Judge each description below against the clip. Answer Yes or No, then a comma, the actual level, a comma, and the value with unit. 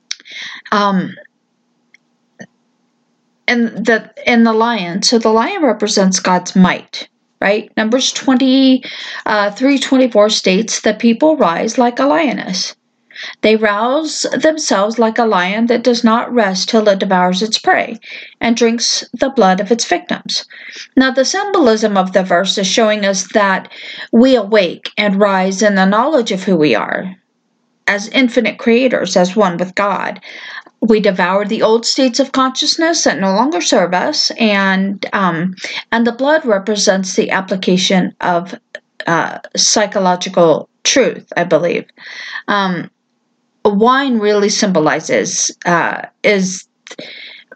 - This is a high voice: Yes, high, 220 Hz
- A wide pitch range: No, average, 4.6 semitones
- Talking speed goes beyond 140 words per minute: No, slow, 135 wpm